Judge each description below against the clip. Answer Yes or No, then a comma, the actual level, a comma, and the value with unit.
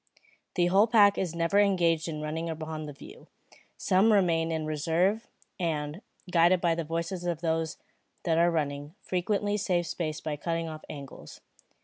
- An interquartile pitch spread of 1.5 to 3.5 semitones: Yes, average, 2.7 semitones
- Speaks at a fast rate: No, average, 160 wpm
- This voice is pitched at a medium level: Yes, medium, 165 Hz